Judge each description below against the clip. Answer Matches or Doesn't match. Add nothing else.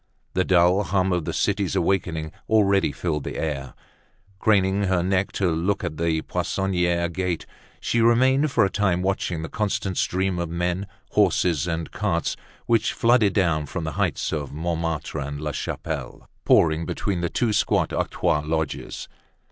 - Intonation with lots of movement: Doesn't match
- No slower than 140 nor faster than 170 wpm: Matches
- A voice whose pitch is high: Doesn't match